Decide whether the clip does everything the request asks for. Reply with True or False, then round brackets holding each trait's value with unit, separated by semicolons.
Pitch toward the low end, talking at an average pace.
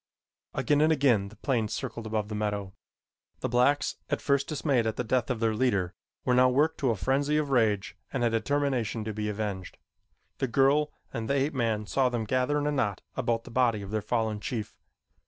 False (120 Hz; 210 wpm)